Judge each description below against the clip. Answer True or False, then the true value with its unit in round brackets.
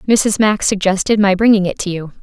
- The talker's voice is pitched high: True (200 Hz)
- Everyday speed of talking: False (215 wpm)